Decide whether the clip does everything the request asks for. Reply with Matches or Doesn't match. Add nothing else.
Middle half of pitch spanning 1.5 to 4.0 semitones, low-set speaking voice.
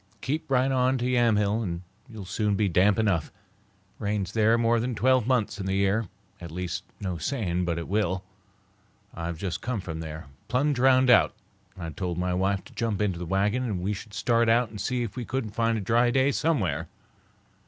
Doesn't match